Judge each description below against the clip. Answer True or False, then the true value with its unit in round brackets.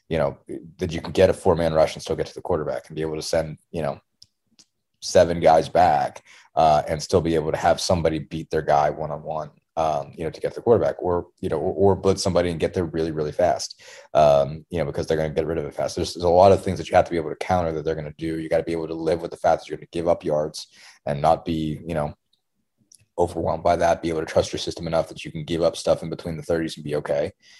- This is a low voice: True (80 Hz)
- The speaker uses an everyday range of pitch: False (1.7 semitones)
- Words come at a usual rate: False (295 wpm)